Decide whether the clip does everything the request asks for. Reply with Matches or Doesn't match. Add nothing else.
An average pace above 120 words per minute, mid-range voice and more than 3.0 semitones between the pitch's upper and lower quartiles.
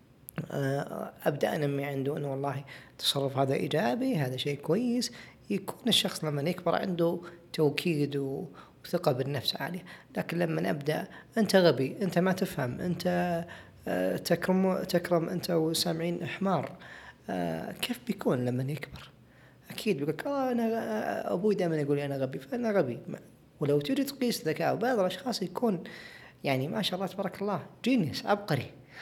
Matches